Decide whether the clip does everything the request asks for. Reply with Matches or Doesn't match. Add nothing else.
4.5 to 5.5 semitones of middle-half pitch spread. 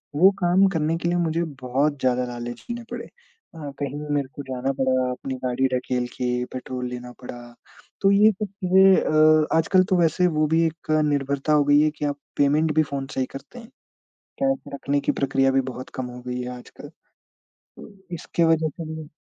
Matches